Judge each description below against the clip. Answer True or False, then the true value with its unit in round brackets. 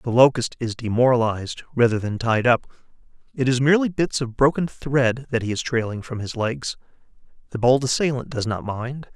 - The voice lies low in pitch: True (125 Hz)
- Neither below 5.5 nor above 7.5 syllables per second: False (5.3 syllables/s)